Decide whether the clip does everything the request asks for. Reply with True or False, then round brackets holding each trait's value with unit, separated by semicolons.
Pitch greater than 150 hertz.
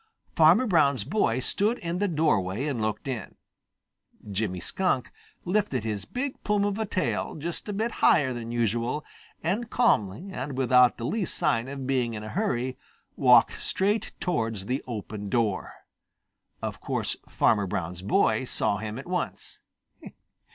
False (130 Hz)